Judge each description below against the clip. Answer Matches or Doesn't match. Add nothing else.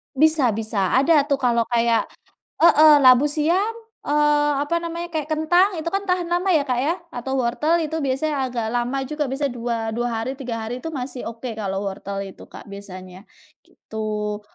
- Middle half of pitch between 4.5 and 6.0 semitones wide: Matches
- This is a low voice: Doesn't match